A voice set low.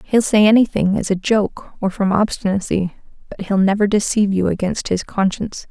No: high, 200 Hz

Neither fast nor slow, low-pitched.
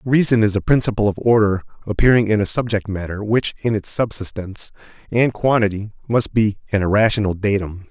Yes: average, 165 wpm; low, 105 Hz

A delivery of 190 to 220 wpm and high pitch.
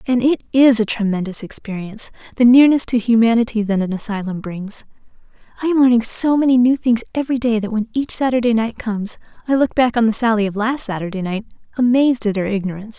Yes: average, 200 wpm; high, 230 Hz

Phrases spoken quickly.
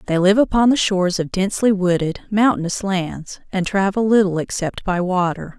No: average, 170 wpm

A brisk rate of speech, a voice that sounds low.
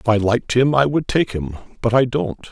Yes: fast, 265 wpm; low, 120 Hz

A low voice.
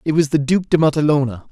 No: medium, 150 Hz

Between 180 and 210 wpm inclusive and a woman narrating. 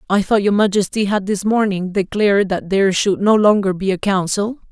No: fast, 205 wpm; male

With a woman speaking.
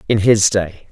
No: male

